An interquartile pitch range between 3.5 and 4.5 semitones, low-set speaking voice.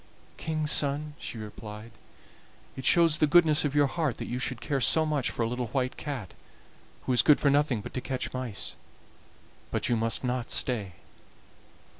Yes: average, 4.0 semitones; low, 130 Hz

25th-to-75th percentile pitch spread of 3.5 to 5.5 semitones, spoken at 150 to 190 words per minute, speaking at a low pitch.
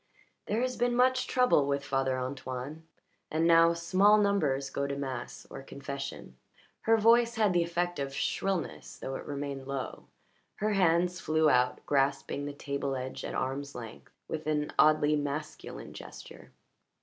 No: average, 4.5 semitones; average, 155 wpm; medium, 150 Hz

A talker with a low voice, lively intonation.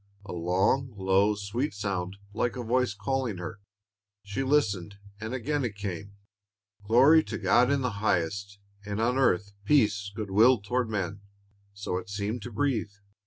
No: low, 105 Hz; average, 3.8 semitones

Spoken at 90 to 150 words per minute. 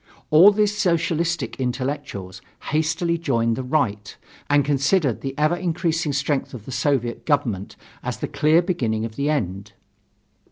Yes: average, 145 wpm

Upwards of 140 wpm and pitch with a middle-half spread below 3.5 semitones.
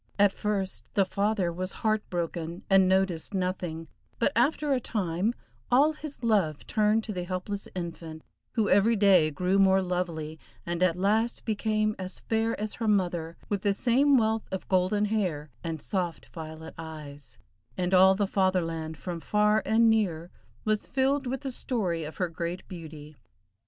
No: average, 165 wpm; average, 4.1 semitones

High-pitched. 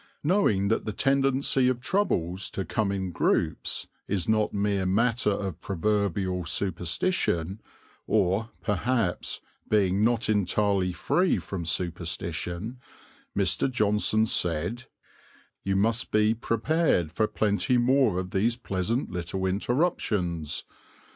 No: low, 100 Hz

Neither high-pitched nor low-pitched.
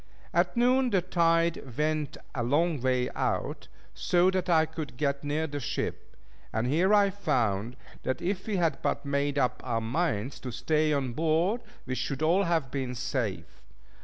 Yes: medium, 150 Hz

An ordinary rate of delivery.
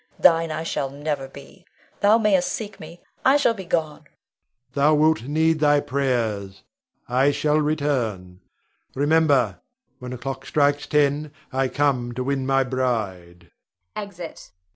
Yes: average, 145 wpm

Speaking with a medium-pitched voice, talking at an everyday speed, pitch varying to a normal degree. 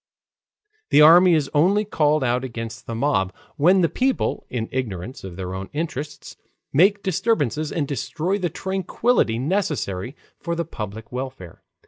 No: medium, 145 Hz; average, 145 wpm; wide, 7.2 semitones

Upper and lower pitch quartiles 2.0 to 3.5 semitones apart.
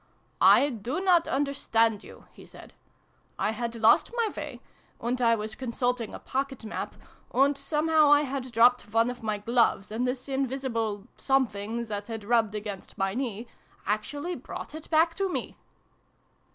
No: average, 3.9 semitones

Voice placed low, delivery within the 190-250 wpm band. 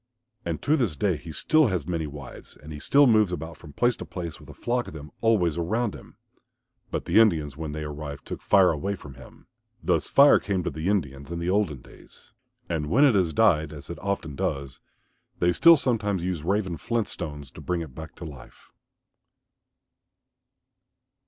Yes: very low, 85 Hz; average, 195 wpm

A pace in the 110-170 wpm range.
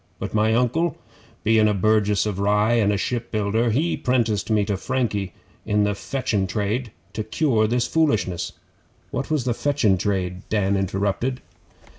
Yes: average, 155 wpm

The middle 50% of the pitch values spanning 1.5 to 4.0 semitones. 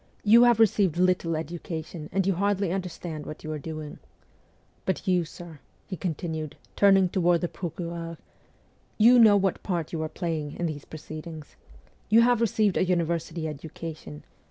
Yes: average, 3.4 semitones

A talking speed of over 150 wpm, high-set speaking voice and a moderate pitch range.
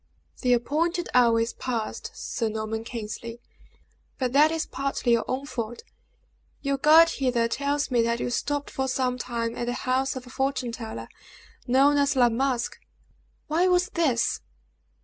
Yes: average, 160 wpm; very high, 255 Hz; average, 3.1 semitones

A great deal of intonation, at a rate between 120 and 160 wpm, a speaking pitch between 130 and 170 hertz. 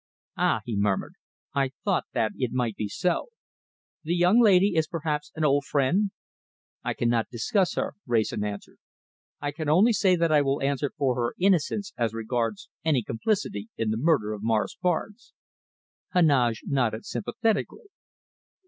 Yes: wide, 7.5 semitones; average, 155 wpm; medium, 140 Hz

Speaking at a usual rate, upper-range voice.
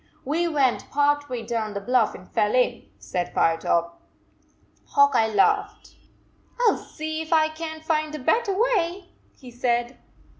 Yes: average, 165 wpm; very high, 285 Hz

